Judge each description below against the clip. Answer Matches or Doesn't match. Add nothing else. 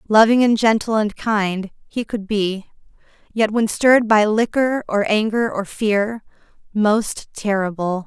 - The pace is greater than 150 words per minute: Doesn't match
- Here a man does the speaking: Doesn't match